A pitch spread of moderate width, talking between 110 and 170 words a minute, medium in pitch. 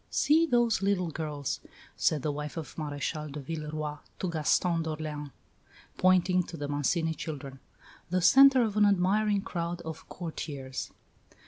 Yes: average, 3.7 semitones; average, 140 wpm; medium, 165 Hz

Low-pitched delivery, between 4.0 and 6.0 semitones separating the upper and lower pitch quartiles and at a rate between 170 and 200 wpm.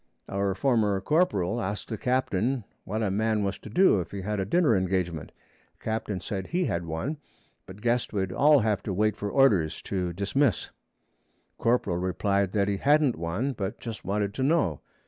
Yes: low, 105 Hz; average, 4.3 semitones; average, 180 wpm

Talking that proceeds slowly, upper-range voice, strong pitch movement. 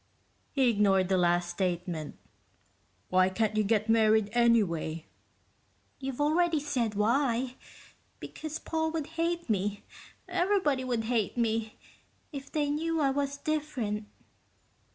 Yes: slow, 120 wpm; high, 235 Hz; wide, 6.0 semitones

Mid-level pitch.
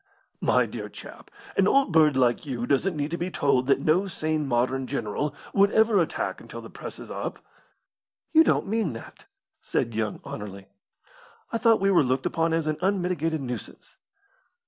Yes: medium, 155 Hz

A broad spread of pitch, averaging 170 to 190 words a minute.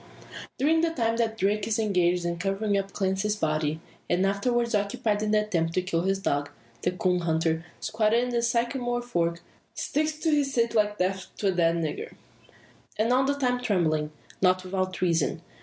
No: average, 4.8 semitones; average, 185 wpm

